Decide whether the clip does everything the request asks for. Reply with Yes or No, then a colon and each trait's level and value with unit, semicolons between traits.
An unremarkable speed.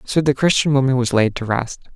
No: fast, 245 wpm